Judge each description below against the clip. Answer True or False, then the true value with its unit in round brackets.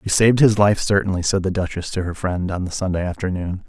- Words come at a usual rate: False (245 wpm)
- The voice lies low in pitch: True (95 Hz)